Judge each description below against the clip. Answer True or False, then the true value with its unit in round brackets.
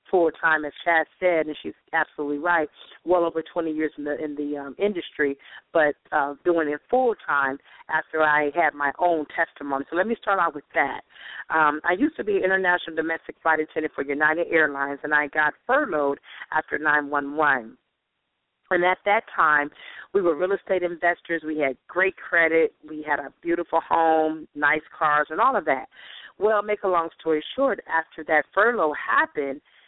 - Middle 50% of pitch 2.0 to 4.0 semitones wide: True (2.9 semitones)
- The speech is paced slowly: False (185 wpm)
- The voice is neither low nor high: True (160 Hz)